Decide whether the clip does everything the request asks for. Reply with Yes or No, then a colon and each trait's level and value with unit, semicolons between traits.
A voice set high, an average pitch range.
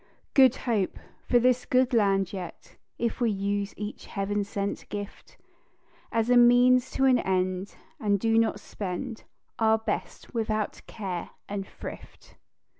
Yes: high, 215 Hz; average, 3.4 semitones